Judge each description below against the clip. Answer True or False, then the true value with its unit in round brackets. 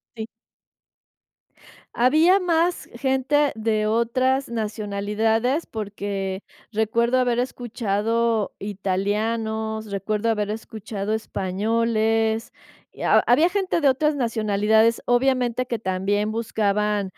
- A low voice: False (225 Hz)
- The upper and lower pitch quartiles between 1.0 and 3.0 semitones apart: True (2.7 semitones)